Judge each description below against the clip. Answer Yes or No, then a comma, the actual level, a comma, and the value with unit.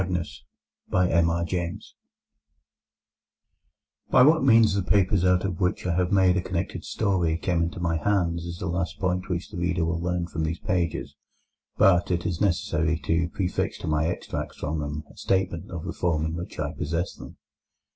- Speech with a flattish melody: Yes, narrow, 1.7 semitones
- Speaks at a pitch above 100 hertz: No, very low, 85 Hz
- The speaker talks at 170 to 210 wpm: Yes, average, 175 wpm